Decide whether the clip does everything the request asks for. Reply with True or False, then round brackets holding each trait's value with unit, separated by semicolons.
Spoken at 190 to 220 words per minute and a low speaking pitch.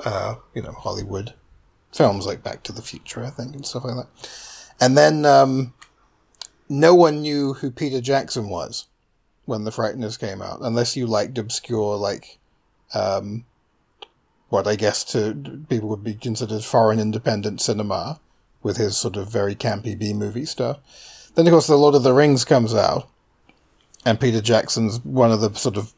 False (175 wpm; 120 Hz)